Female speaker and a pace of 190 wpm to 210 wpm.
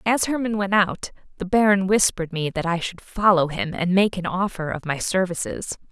Yes: female; fast, 205 wpm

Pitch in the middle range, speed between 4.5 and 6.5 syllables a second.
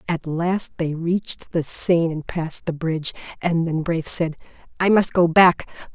Yes: medium, 165 Hz; 4.6 syllables/s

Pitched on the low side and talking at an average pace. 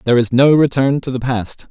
No: low, 130 Hz; fast, 245 wpm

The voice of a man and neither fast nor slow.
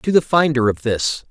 No: male; fast, 230 wpm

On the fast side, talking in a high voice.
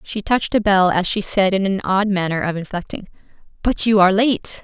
Yes: fast, 220 wpm; high, 195 Hz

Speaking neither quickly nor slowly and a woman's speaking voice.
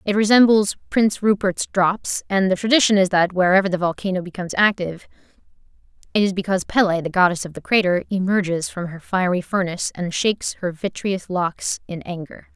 Yes: average, 170 wpm; female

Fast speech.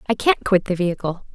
Yes: fast, 225 wpm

